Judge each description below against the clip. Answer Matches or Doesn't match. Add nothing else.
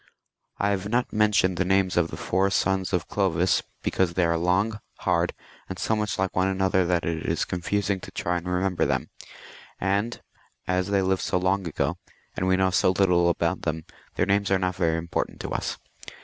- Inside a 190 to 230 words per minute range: Matches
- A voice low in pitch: Matches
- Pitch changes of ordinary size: Doesn't match